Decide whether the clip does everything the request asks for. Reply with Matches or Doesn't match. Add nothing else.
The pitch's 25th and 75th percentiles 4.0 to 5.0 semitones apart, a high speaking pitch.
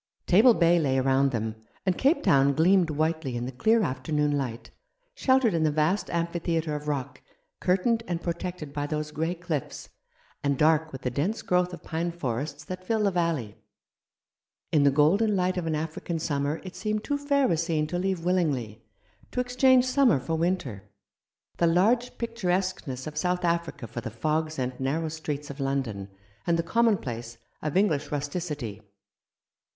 Doesn't match